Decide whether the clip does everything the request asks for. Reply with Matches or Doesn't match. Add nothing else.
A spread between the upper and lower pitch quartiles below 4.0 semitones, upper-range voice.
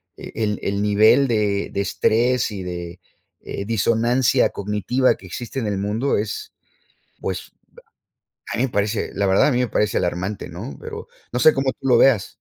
Doesn't match